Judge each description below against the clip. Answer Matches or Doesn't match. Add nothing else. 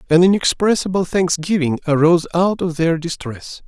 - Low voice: Doesn't match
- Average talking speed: Doesn't match